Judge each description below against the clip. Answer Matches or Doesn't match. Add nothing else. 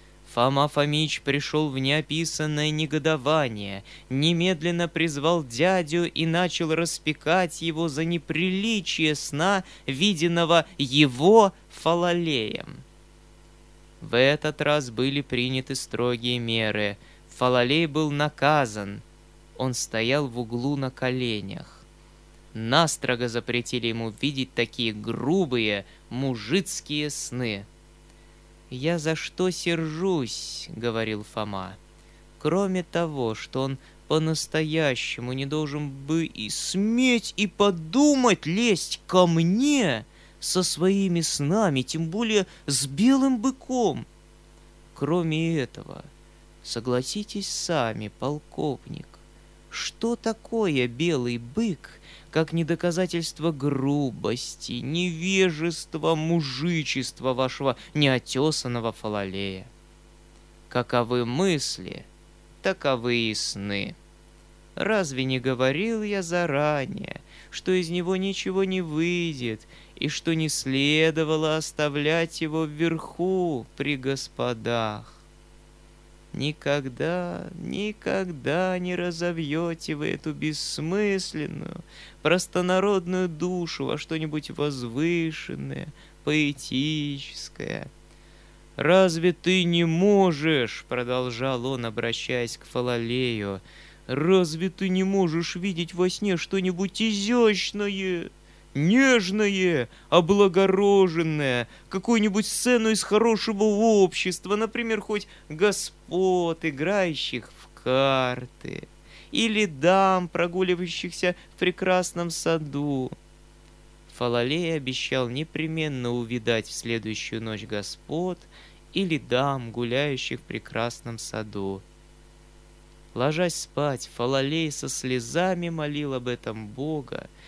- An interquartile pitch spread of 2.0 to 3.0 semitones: Doesn't match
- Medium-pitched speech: Matches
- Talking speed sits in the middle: Doesn't match